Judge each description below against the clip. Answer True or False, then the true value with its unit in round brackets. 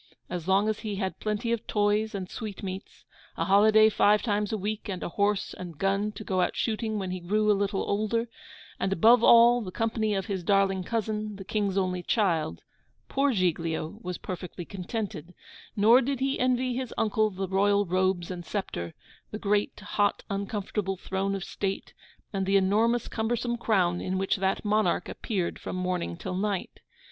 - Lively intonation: False (2.5 semitones)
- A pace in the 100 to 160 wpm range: False (180 wpm)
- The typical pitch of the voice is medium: False (200 Hz)